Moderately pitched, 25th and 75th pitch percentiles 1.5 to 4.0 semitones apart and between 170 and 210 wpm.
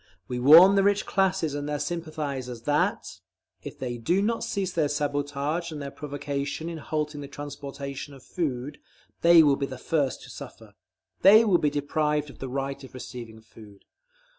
Yes: medium, 145 Hz; average, 2.9 semitones; average, 175 wpm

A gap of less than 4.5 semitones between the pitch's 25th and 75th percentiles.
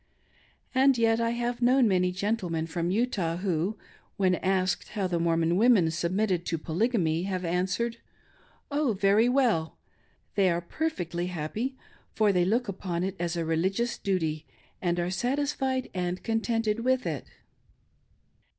No: average, 5.1 semitones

